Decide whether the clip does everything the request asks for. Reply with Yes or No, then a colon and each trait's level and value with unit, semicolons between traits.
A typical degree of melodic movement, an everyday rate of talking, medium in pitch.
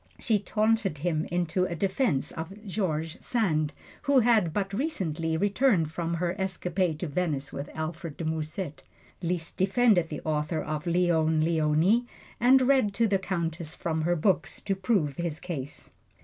Yes: average, 4.0 semitones; average, 155 wpm; medium, 175 Hz